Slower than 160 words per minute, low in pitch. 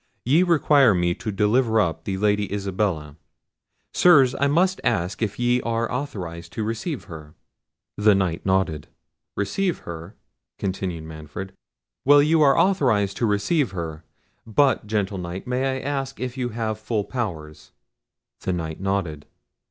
Yes: average, 145 wpm; low, 105 Hz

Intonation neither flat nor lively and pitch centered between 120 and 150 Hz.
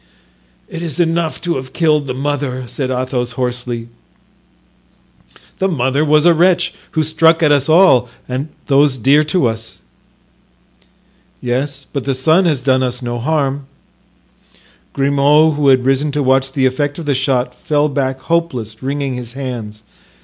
Yes: average, 3.1 semitones; medium, 140 Hz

